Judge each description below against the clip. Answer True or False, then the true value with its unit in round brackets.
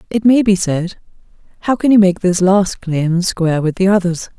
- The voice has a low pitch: False (185 Hz)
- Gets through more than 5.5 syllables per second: False (4.9 syllables/s)